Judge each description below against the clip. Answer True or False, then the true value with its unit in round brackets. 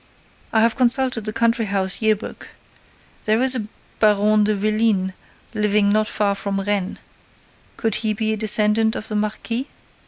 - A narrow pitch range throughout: True (1.5 semitones)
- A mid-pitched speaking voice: False (215 Hz)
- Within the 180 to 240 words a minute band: False (160 wpm)